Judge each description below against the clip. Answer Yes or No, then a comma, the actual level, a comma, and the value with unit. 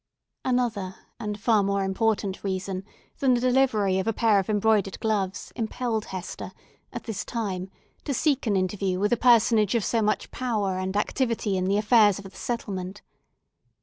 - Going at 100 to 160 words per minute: No, average, 170 wpm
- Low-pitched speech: No, high, 210 Hz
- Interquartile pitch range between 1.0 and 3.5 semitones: Yes, average, 3.1 semitones